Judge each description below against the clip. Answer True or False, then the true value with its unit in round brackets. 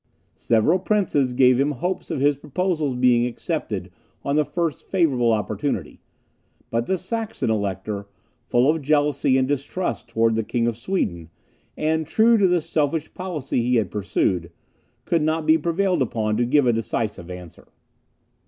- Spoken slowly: False (155 wpm)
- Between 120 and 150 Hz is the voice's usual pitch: True (135 Hz)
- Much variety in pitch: True (6.0 semitones)